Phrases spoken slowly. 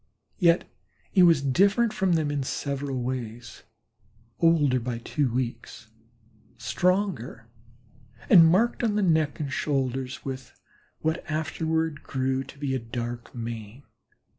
Yes: slow, 125 wpm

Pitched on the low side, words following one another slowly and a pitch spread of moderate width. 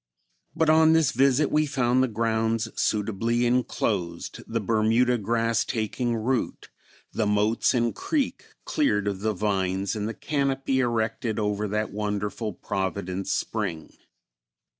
Yes: low, 110 Hz; slow, 130 wpm; average, 3.2 semitones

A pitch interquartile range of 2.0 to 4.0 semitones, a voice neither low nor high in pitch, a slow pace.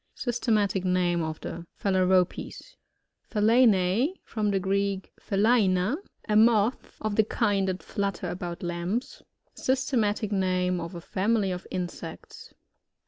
No: average, 3.1 semitones; high, 195 Hz; slow, 120 wpm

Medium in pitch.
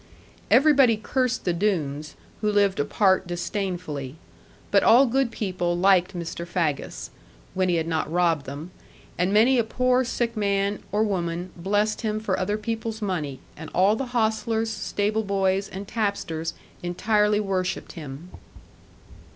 No: high, 195 Hz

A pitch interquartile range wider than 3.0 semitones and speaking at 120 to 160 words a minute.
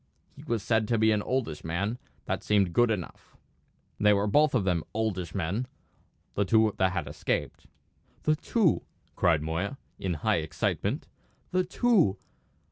Yes: average, 4.9 semitones; average, 155 wpm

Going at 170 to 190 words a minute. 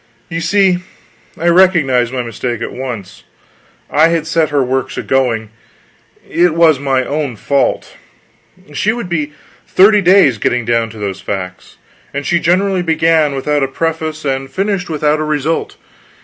No: average, 155 wpm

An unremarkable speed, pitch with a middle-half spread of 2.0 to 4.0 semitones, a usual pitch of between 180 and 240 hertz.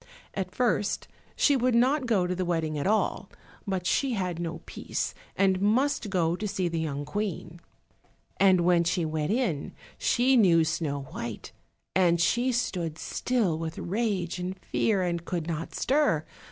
No: average, 165 wpm; average, 4.6 semitones; medium, 185 Hz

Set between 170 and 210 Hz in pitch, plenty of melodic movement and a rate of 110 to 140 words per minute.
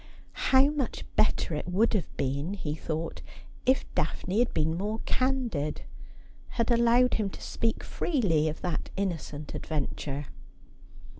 Yes: high, 190 Hz; wide, 7.3 semitones; slow, 135 wpm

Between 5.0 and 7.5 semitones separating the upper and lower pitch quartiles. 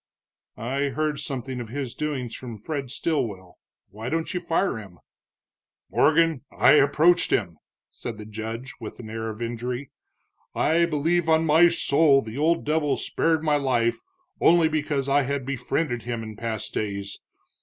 Yes: average, 5.3 semitones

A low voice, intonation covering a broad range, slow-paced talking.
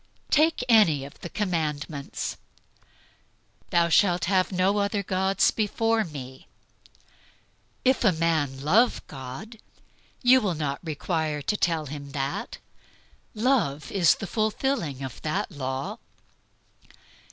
No: medium, 170 Hz; wide, 6.4 semitones; slow, 115 wpm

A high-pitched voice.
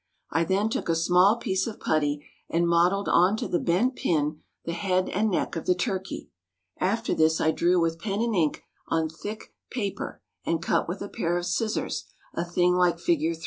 No: medium, 175 Hz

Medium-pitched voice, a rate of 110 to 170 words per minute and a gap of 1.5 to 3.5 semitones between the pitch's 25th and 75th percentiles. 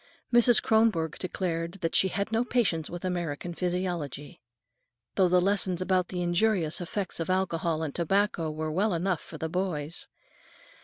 Yes: medium, 180 Hz; average, 155 wpm; average, 2.7 semitones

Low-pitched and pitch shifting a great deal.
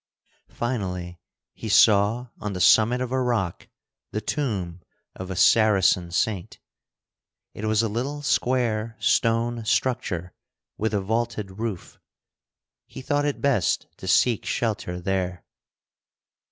No: low, 110 Hz; average, 4.0 semitones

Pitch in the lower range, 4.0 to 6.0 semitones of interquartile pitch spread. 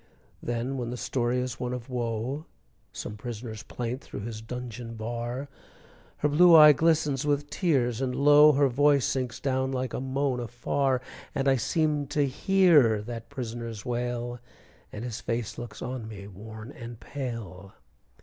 No: low, 125 Hz; average, 3.2 semitones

